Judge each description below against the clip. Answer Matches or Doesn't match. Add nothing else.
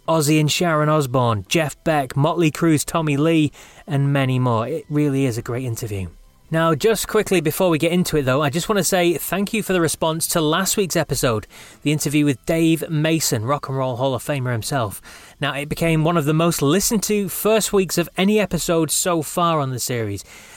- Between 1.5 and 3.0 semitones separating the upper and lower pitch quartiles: Doesn't match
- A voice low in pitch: Doesn't match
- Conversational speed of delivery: Doesn't match